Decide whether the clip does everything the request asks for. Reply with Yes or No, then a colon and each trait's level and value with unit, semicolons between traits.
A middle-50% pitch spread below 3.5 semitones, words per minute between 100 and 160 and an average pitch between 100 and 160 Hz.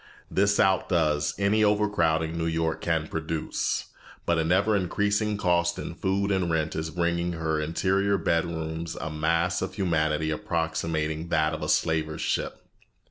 No: average, 2.9 semitones; average, 150 wpm; very low, 85 Hz